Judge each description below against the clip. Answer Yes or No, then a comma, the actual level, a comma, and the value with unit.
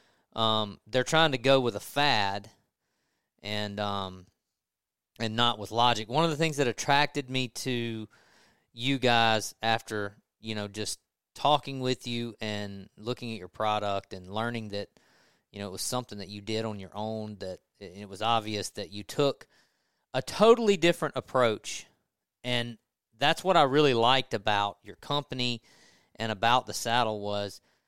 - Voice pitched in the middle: No, low, 115 Hz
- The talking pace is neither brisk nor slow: Yes, average, 160 wpm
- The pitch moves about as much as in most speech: Yes, average, 3.7 semitones